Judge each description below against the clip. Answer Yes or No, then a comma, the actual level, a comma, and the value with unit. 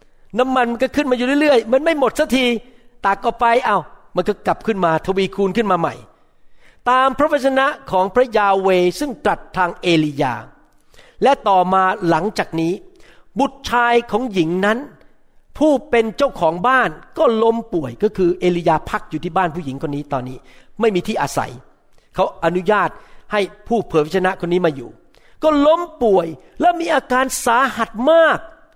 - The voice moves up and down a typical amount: No, wide, 6.3 semitones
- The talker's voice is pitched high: Yes, high, 215 Hz